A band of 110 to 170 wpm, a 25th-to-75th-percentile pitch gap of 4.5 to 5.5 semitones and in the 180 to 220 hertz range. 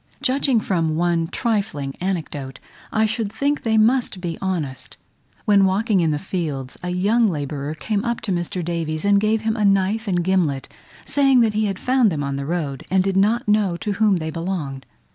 No: average, 195 wpm; average, 5.1 semitones; high, 190 Hz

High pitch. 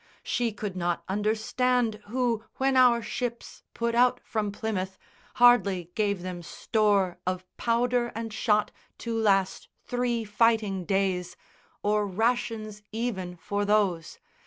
Yes: high, 215 Hz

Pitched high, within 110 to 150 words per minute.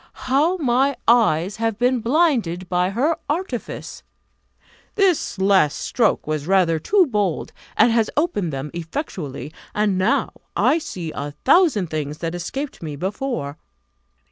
Yes: high, 205 Hz; slow, 135 wpm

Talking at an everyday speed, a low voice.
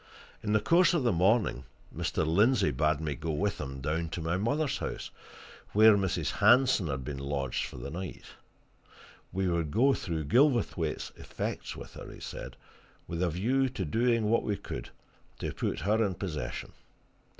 Yes: average, 170 wpm; very low, 95 Hz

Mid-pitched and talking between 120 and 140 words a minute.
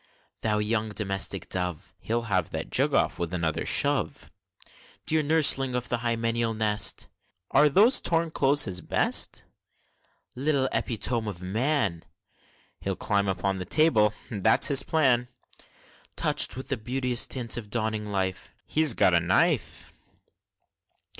No: low, 115 Hz; slow, 135 wpm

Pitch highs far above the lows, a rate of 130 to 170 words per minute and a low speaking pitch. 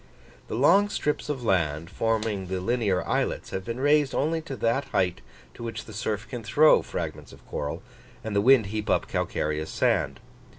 No: wide, 6.0 semitones; average, 180 wpm; low, 110 Hz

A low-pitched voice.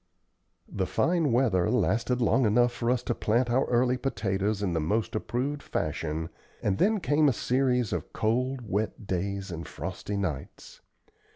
Yes: low, 115 Hz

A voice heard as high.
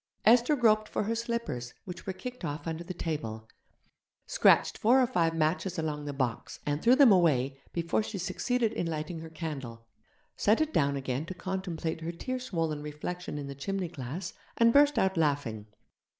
No: medium, 170 Hz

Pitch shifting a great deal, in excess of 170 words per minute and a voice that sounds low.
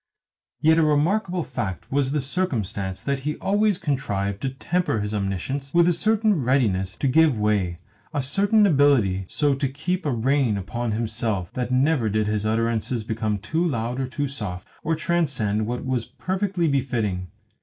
No: wide, 6.4 semitones; average, 165 wpm; low, 130 Hz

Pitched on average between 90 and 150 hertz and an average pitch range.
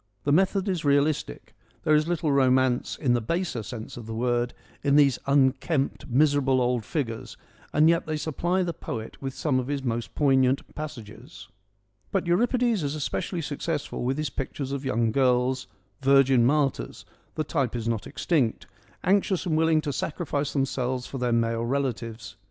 Yes: low, 135 Hz; average, 3.9 semitones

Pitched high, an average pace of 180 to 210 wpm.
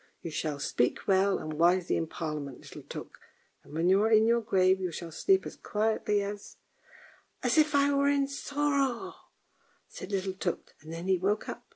Yes: high, 195 Hz; fast, 205 wpm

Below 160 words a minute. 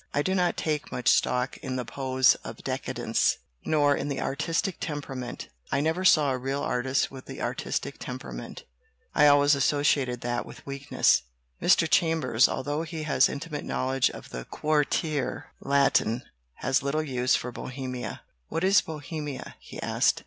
No: average, 165 wpm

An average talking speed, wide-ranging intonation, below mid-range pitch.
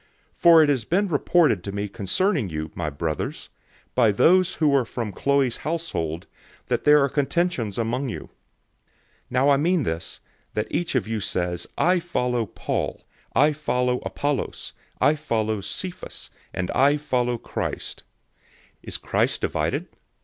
Yes: average, 155 wpm; wide, 6.4 semitones; low, 125 Hz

